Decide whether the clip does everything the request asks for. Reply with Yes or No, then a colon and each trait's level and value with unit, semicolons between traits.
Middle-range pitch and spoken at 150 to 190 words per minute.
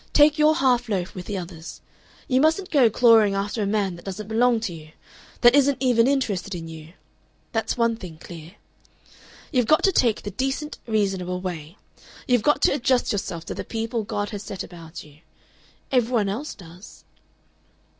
No: high, 215 Hz; average, 180 wpm